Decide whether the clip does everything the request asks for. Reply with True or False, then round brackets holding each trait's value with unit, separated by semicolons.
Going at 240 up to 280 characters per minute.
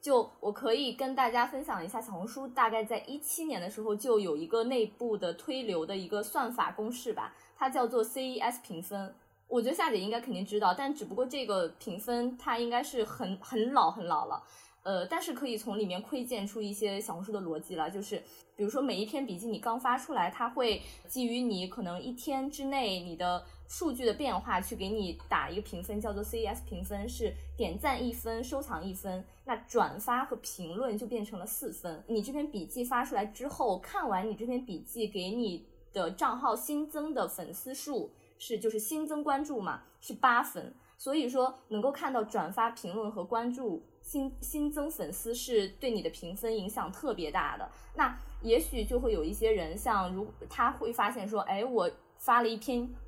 False (295 characters per minute)